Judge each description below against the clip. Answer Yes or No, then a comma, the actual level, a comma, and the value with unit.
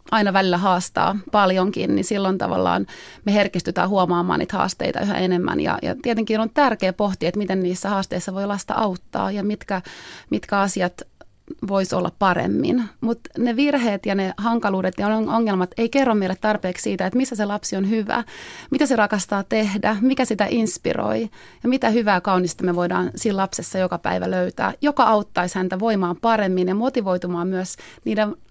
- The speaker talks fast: Yes, fast, 170 wpm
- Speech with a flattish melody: No, average, 3.3 semitones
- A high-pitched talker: Yes, high, 200 Hz